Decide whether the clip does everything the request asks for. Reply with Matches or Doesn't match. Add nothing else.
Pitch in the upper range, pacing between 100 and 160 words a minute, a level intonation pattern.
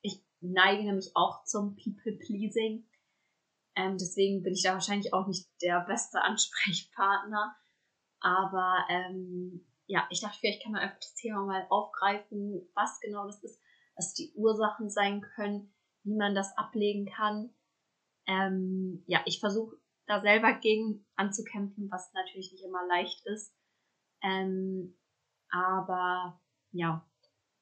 Matches